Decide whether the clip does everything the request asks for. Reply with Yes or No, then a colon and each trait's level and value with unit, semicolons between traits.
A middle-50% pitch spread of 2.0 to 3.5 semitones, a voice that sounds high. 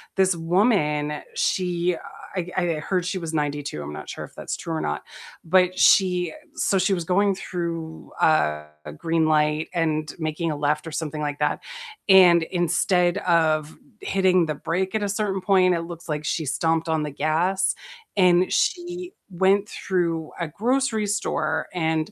No: average, 3.1 semitones; medium, 170 Hz